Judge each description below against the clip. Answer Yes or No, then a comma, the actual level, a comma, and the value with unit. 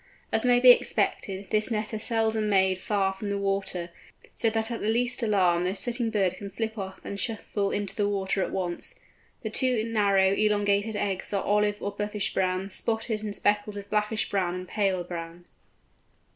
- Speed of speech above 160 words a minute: Yes, average, 185 wpm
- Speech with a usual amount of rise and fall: No, narrow, 2.3 semitones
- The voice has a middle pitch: No, high, 205 Hz